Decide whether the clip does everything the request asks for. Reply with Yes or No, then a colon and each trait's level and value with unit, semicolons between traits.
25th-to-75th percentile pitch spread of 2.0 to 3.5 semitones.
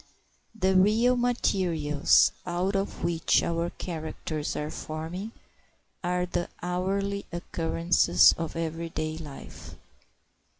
Yes: average, 2.9 semitones